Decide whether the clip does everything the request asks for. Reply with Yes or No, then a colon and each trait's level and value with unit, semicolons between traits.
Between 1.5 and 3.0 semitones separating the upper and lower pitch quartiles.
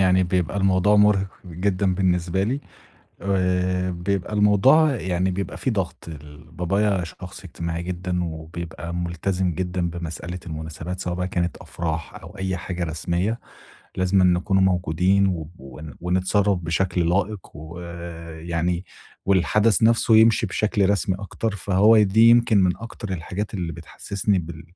Yes: narrow, 2.5 semitones